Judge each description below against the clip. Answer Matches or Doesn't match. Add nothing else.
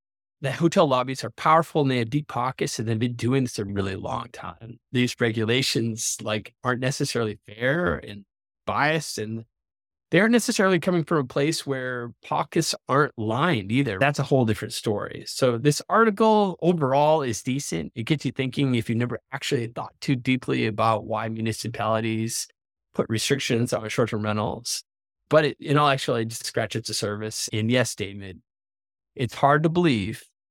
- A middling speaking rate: Matches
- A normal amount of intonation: Matches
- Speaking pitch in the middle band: Doesn't match